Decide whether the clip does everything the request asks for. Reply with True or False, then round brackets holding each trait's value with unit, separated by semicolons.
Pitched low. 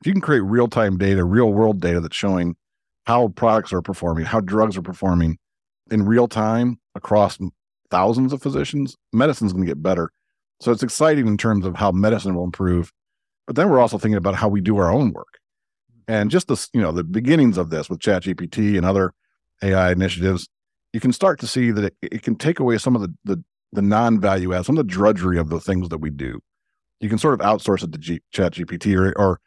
True (105 Hz)